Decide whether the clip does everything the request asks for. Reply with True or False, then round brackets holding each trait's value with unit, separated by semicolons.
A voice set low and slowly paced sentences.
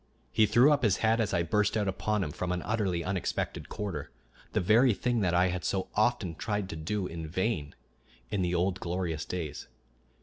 False (95 Hz; 200 wpm)